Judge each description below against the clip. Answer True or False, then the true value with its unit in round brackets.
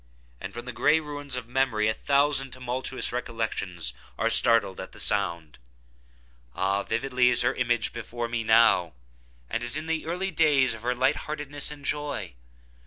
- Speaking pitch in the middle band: False (125 Hz)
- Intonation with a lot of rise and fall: False (4.2 semitones)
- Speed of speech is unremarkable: True (165 wpm)